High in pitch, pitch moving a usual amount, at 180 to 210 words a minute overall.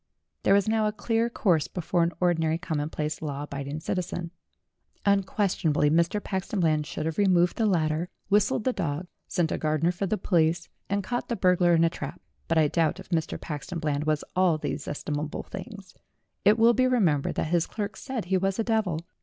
No: medium, 175 Hz; average, 4.3 semitones; average, 195 wpm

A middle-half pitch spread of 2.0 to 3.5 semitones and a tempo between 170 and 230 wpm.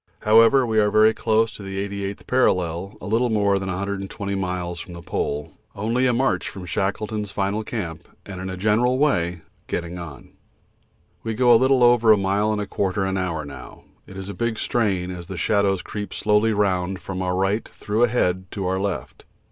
Yes: average, 2.9 semitones; average, 190 wpm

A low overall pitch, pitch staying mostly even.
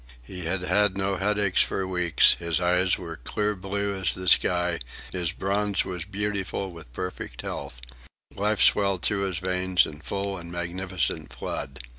Yes: very low, 95 Hz; narrow, 2.1 semitones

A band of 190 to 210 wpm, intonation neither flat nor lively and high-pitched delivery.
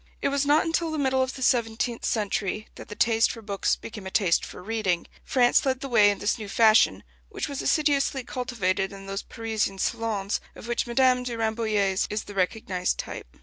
Yes: average, 200 wpm; average, 4.0 semitones; high, 225 Hz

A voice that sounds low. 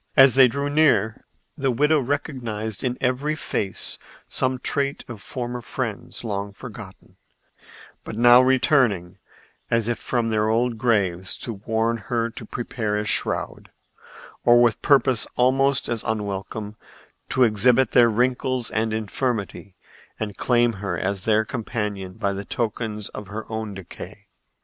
Yes: low, 115 Hz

